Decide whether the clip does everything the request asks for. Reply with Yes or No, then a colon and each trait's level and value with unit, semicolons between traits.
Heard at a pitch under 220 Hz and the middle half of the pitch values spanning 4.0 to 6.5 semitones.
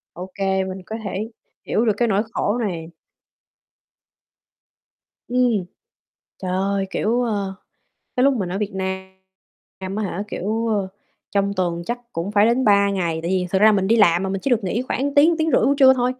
No: high, 200 Hz; average, 3.5 semitones